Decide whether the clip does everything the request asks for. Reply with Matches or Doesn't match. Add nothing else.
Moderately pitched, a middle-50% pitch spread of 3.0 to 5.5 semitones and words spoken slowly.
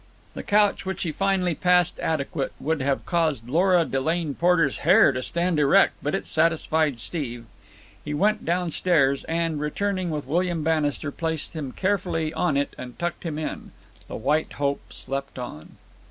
Doesn't match